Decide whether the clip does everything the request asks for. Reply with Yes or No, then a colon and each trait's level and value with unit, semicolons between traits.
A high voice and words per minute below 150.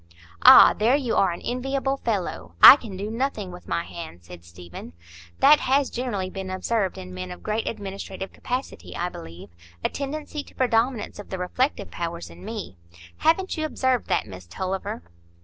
No: high, 195 Hz; average, 170 wpm